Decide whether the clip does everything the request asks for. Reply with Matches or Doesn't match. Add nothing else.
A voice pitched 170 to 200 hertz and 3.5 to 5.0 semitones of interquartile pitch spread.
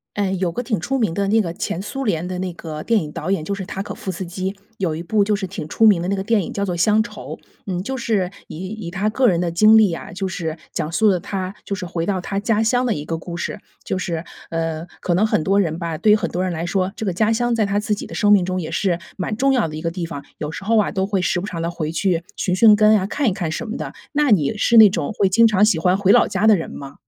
Matches